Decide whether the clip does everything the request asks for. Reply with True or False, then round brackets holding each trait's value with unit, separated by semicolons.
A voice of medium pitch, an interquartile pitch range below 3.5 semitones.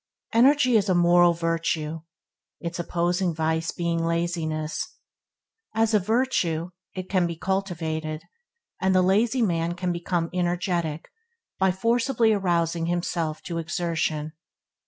True (175 Hz; 2.4 semitones)